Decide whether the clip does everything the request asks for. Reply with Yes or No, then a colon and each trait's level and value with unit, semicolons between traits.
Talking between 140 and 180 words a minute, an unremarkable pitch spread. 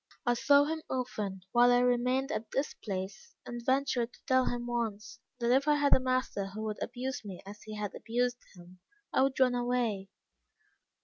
No: average, 190 wpm; average, 3.4 semitones